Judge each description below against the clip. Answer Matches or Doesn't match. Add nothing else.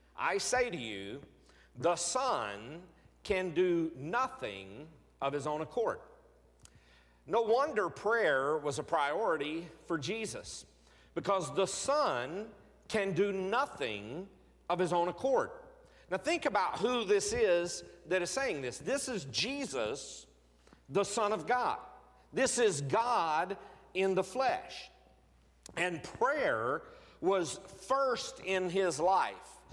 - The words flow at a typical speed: Doesn't match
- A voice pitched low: Doesn't match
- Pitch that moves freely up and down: Matches